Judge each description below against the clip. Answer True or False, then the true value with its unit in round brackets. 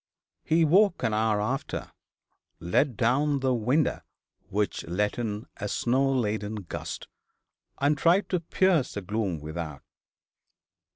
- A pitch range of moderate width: False (5.8 semitones)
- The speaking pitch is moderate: False (115 Hz)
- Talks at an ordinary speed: False (125 wpm)